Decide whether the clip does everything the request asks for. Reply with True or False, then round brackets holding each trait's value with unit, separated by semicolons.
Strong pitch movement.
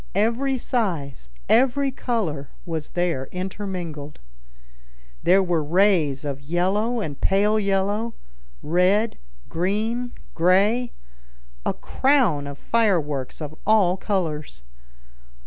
True (6.5 semitones)